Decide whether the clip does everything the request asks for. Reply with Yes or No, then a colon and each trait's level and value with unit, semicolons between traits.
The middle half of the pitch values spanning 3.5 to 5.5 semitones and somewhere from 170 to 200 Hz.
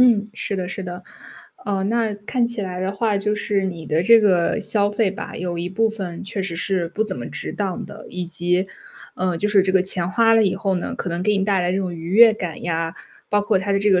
No: narrow, 2.6 semitones; high, 195 Hz